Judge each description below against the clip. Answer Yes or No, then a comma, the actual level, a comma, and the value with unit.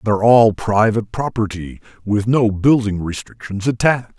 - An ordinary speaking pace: No, slow, 130 wpm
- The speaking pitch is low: Yes, low, 110 Hz